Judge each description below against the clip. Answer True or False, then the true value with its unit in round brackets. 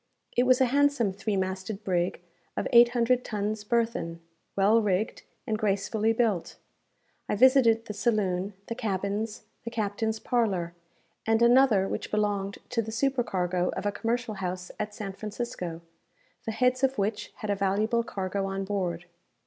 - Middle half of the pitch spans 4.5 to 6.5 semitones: False (3.2 semitones)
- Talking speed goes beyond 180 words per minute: False (155 wpm)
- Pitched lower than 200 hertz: False (210 Hz)